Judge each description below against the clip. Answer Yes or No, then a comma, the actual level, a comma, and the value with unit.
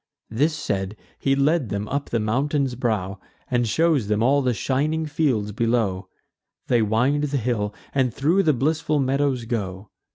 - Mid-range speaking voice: No, low, 125 Hz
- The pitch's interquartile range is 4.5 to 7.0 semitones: Yes, average, 5.1 semitones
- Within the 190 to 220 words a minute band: No, average, 160 wpm